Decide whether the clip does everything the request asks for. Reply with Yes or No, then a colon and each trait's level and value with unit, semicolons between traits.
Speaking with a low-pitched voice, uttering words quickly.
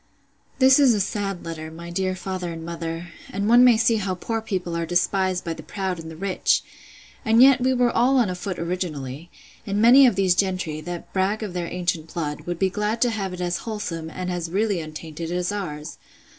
No: medium, 185 Hz; fast, 215 wpm